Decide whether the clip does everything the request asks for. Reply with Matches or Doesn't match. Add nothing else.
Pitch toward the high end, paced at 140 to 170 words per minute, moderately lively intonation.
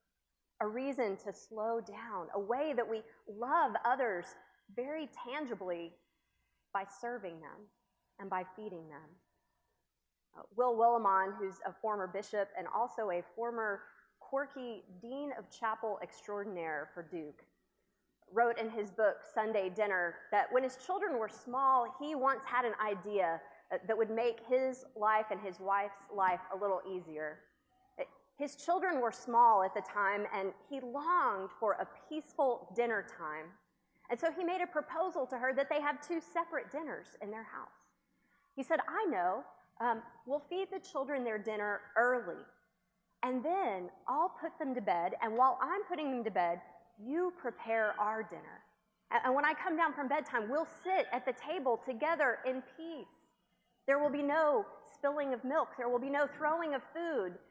Doesn't match